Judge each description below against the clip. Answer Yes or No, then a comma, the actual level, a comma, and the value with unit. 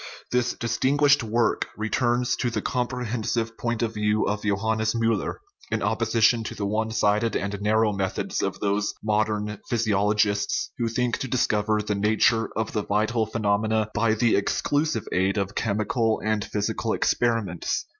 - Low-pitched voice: Yes, low, 110 Hz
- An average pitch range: No, narrow, 1.9 semitones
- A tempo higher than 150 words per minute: Yes, average, 160 wpm